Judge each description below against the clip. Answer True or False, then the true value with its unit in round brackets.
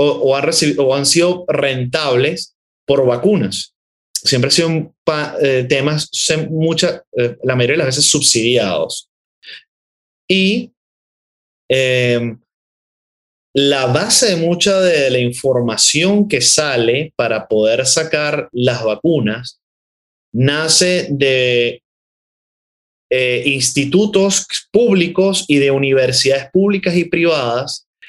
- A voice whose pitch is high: False (140 Hz)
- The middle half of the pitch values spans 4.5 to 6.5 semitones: True (5.2 semitones)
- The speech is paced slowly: True (110 wpm)